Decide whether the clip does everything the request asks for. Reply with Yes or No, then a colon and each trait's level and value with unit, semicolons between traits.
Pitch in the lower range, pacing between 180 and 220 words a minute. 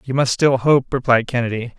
Yes: low, 125 Hz; average, 200 wpm